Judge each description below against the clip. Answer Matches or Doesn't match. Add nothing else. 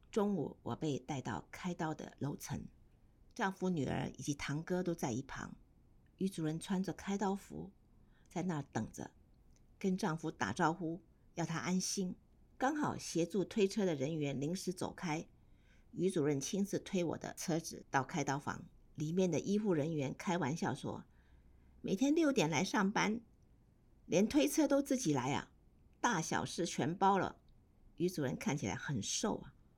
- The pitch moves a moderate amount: Matches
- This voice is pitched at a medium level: Matches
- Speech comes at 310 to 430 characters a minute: Doesn't match